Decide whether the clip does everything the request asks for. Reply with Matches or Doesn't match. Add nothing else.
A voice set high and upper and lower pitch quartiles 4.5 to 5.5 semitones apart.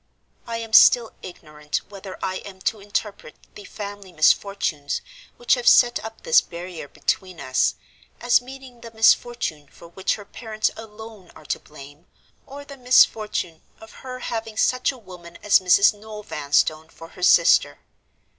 Matches